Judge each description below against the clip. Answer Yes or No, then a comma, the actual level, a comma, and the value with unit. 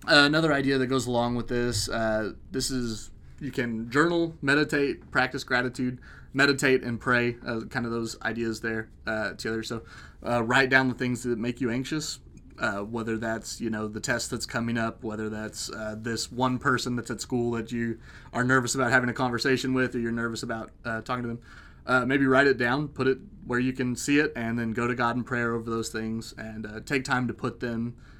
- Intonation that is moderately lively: No, narrow, 2.2 semitones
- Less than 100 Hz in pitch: No, low, 120 Hz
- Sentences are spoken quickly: Yes, fast, 220 wpm